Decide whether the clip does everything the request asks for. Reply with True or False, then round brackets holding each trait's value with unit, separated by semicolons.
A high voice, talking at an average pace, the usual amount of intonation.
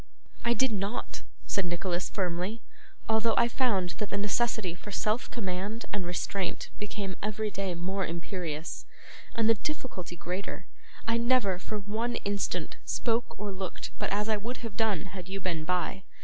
True (200 Hz; 165 wpm; 3.4 semitones)